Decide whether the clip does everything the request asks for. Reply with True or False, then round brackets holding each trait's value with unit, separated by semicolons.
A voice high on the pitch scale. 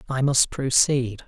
False (130 Hz)